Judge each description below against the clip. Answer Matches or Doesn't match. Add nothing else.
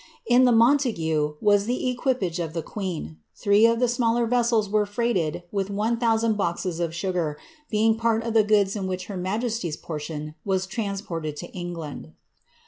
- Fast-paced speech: Doesn't match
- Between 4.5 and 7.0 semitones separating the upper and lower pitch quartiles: Matches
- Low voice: Doesn't match